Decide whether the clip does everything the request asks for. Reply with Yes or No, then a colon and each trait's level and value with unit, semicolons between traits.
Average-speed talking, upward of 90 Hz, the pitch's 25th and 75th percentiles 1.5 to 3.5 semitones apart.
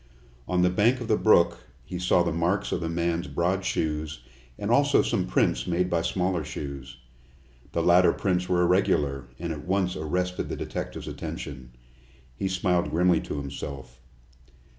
No: average, 160 wpm; very low, 85 Hz; average, 3.0 semitones